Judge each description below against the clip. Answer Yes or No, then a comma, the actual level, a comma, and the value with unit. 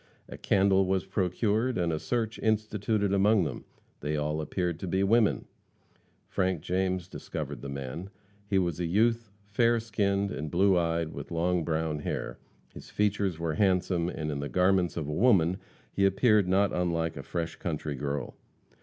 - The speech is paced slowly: No, average, 170 wpm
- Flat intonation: No, average, 3.6 semitones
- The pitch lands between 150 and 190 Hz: No, very low, 90 Hz